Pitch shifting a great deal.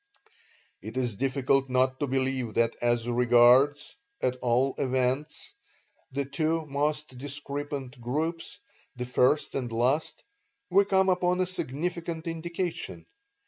No: average, 4.0 semitones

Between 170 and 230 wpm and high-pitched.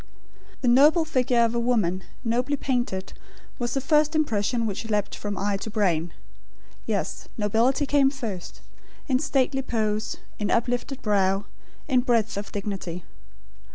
No: average, 140 wpm; high, 235 Hz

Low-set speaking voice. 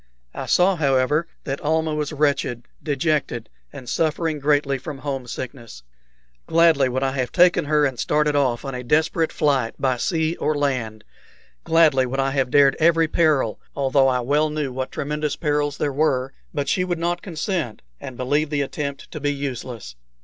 No: medium, 145 Hz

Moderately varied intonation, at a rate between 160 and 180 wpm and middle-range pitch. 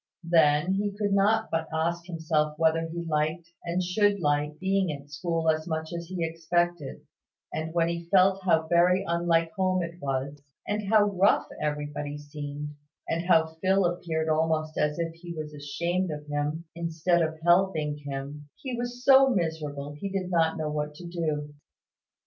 Yes: average, 3.0 semitones; average, 170 wpm; medium, 165 Hz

